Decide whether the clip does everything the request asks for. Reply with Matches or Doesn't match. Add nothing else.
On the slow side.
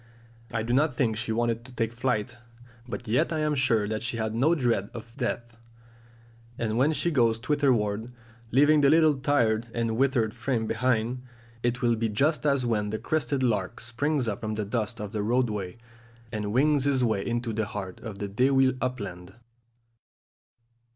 Doesn't match